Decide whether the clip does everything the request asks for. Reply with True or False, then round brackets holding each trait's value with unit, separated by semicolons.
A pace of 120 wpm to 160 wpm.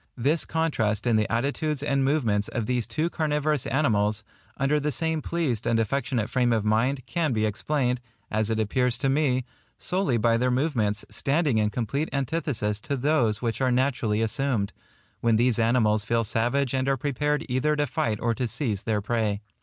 False (180 wpm)